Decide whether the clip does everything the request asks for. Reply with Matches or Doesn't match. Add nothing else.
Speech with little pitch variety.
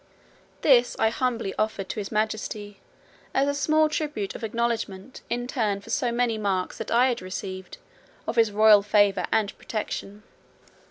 Doesn't match